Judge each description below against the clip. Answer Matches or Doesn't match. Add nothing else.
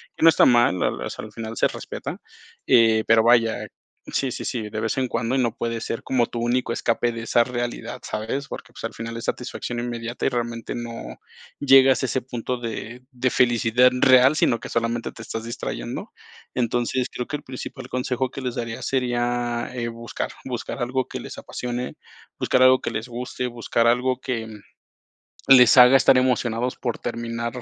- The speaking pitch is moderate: Doesn't match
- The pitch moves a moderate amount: Doesn't match